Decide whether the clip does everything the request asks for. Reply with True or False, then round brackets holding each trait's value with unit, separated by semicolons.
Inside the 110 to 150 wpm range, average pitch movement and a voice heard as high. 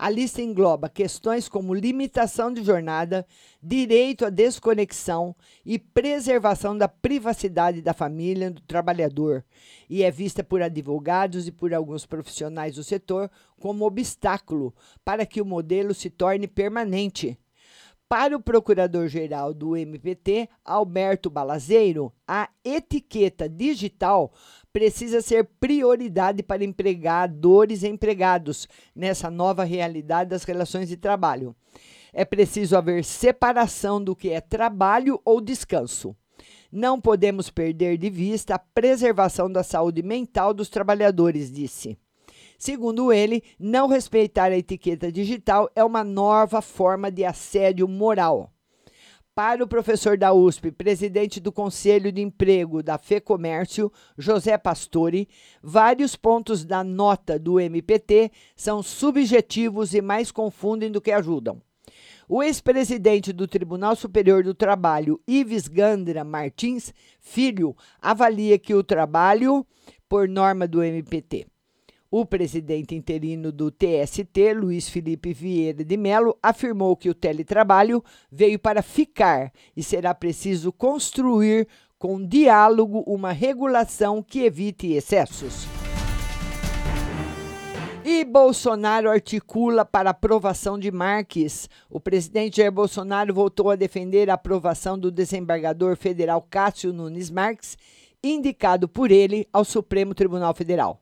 True (120 wpm; 3.9 semitones; 200 Hz)